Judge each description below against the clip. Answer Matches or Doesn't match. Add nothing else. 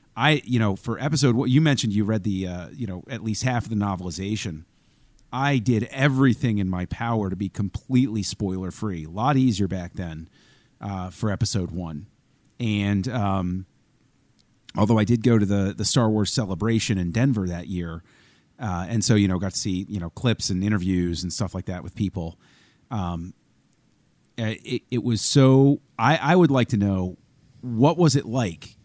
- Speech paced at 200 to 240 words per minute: Doesn't match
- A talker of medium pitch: Doesn't match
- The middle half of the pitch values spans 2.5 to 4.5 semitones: Doesn't match